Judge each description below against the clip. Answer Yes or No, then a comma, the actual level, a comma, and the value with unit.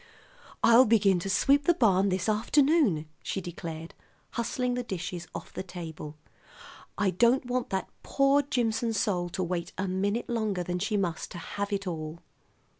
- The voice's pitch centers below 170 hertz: No, high, 200 Hz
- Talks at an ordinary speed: Yes, average, 165 wpm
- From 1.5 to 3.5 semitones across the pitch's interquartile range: No, average, 4.9 semitones